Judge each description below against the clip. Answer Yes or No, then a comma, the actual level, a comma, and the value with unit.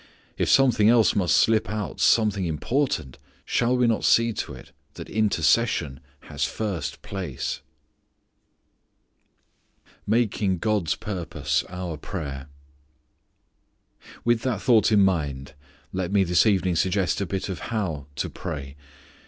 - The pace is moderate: No, slow, 125 wpm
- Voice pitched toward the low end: Yes, very low, 95 Hz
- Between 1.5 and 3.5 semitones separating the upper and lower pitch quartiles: No, average, 4.8 semitones